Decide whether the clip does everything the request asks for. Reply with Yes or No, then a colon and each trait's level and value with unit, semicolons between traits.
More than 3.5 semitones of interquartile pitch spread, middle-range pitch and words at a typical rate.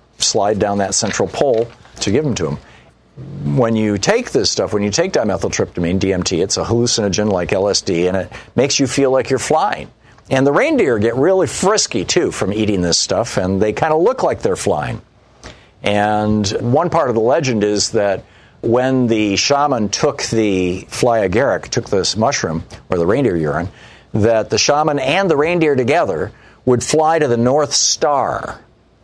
No: average, 4.0 semitones; low, 105 Hz; average, 180 wpm